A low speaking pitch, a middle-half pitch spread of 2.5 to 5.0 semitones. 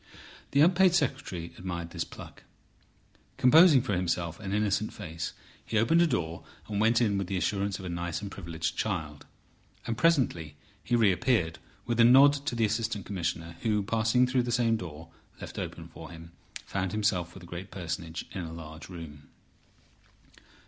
No: low, 100 Hz; wide, 5.5 semitones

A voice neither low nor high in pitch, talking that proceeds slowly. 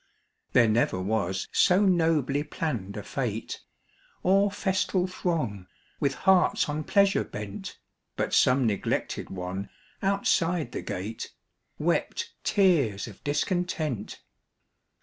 Yes: medium, 145 Hz; slow, 110 wpm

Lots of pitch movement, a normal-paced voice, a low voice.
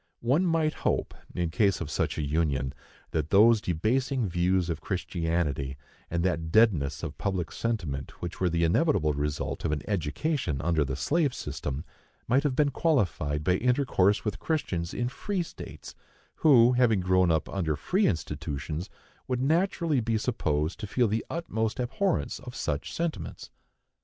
Yes: wide, 8.1 semitones; average, 155 wpm; very low, 95 Hz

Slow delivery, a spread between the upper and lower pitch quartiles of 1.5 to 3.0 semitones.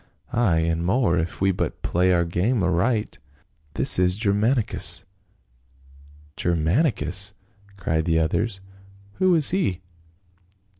No: slow, 120 wpm; average, 4.8 semitones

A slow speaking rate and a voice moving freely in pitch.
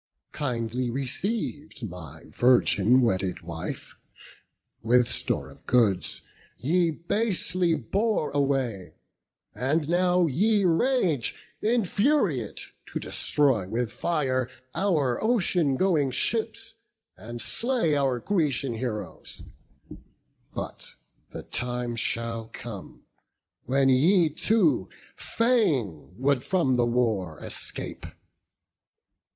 Yes: slow, 95 wpm; wide, 6.9 semitones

